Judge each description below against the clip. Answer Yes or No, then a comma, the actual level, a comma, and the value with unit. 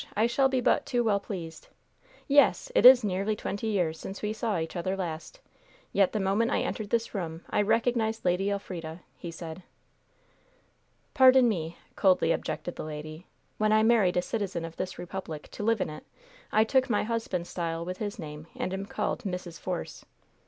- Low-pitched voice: No, high, 195 Hz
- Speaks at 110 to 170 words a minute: No, average, 185 wpm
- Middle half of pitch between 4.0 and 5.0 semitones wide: Yes, average, 4.5 semitones